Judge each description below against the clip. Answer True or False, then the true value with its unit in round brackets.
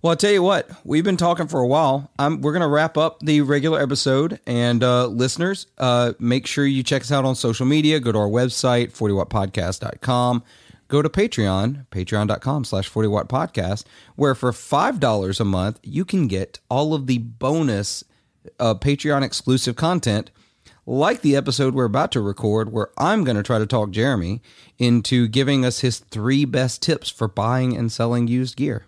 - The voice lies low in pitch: True (125 Hz)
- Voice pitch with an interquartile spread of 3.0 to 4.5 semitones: True (4.2 semitones)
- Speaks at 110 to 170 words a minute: False (185 wpm)